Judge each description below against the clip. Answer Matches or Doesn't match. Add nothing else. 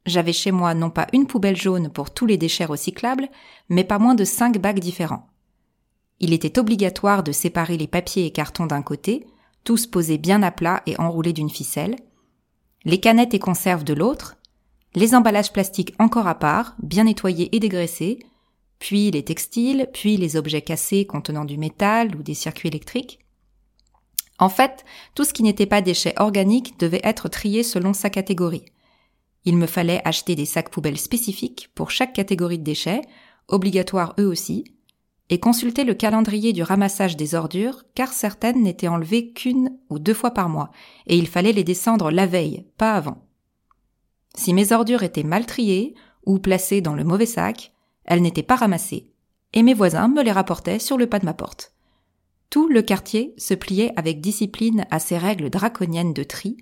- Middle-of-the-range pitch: Doesn't match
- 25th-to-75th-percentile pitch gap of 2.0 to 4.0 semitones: Doesn't match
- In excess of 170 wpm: Matches